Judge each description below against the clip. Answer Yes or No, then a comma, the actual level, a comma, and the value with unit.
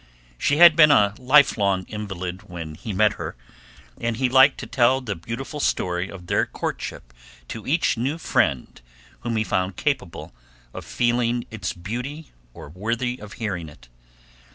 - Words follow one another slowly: No, average, 155 wpm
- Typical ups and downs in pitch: No, wide, 5.8 semitones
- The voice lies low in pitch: Yes, low, 110 Hz